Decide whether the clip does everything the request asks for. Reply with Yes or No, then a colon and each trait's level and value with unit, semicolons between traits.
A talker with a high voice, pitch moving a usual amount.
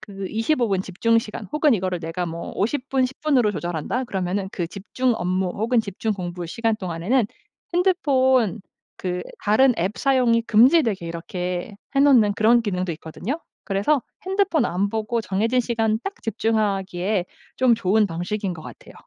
Yes: high, 215 Hz; average, 5.0 semitones